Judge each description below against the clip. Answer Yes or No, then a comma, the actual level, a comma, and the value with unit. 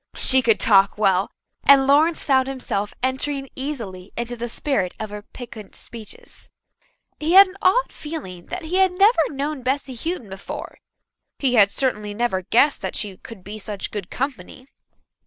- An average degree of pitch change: No, wide, 5.9 semitones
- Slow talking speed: No, average, 165 wpm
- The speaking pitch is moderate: No, very high, 250 Hz